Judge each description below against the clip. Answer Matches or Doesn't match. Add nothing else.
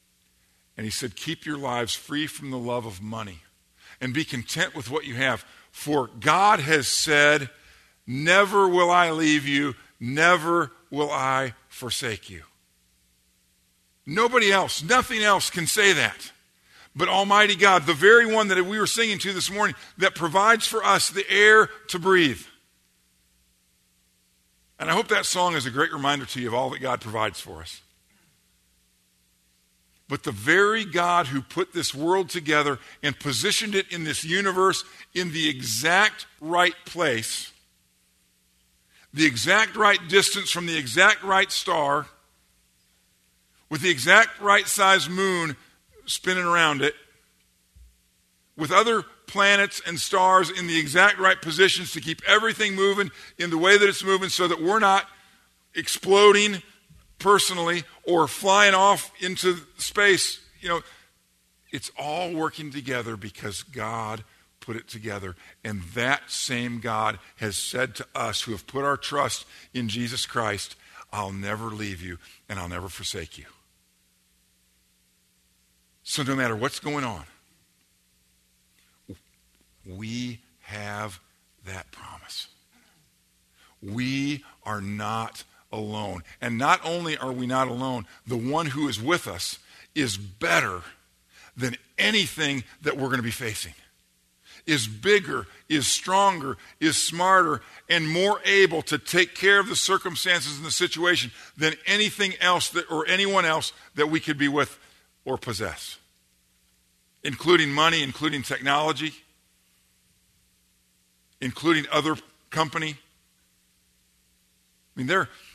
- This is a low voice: Doesn't match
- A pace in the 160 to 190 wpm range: Doesn't match